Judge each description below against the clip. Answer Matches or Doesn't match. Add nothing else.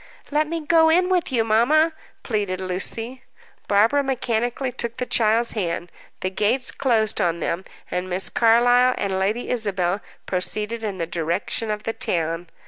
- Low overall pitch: Doesn't match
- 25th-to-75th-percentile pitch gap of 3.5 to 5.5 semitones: Matches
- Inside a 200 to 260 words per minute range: Doesn't match